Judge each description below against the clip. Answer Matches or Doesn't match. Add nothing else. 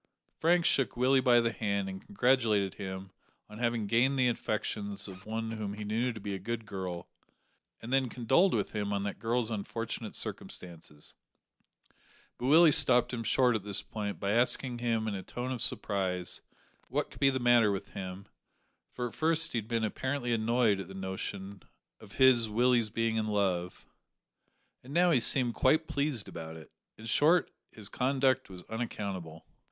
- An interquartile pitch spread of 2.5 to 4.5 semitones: Matches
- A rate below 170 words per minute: Doesn't match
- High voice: Doesn't match